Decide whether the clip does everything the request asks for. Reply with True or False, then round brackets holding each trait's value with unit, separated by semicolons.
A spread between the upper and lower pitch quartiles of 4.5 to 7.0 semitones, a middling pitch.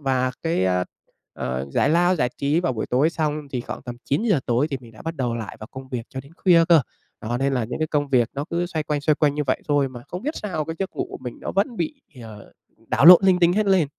True (5.4 semitones; 145 Hz)